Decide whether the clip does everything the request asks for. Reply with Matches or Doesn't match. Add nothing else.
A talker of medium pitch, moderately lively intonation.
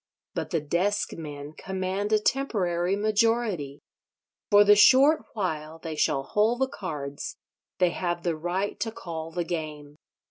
Matches